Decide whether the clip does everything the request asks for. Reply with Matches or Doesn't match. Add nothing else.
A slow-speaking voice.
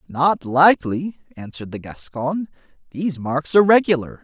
Matches